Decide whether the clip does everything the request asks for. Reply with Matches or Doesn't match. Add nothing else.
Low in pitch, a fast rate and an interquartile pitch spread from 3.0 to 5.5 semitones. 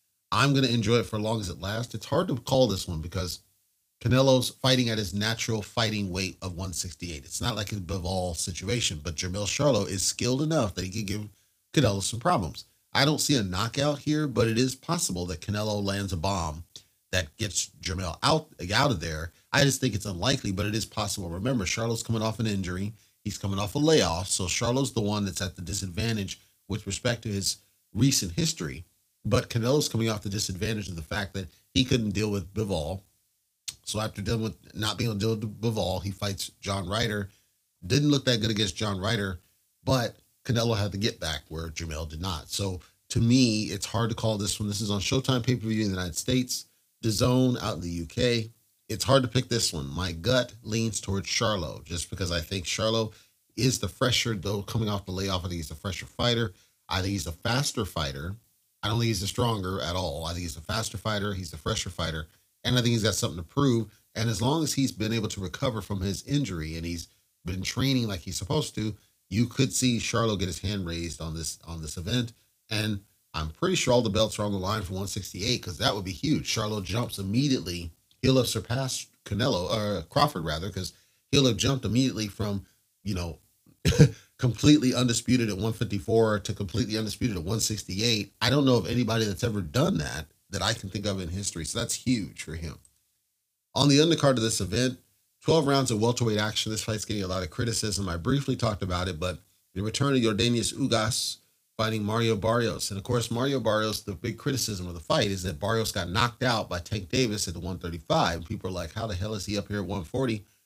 Matches